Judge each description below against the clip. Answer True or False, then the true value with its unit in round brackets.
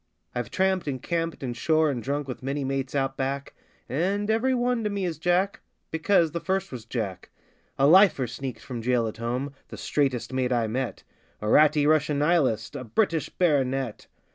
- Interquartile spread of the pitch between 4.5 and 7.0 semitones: True (5.1 semitones)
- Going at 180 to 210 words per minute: True (185 wpm)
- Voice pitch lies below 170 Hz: True (140 Hz)